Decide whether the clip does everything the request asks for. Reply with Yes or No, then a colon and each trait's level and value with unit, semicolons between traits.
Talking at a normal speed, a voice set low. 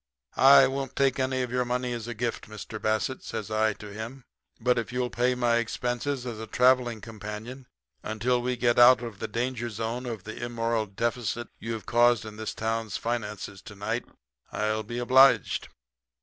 Yes: average, 185 wpm; low, 120 Hz